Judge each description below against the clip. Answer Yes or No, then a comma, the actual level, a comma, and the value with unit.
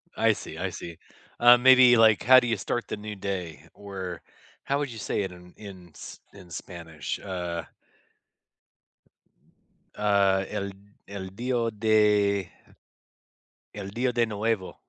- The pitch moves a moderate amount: Yes, average, 3.7 semitones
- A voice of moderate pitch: No, low, 100 Hz